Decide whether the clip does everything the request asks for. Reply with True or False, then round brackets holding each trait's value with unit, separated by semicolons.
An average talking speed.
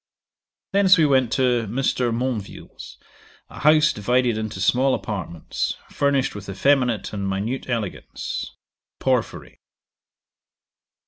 False (105 wpm)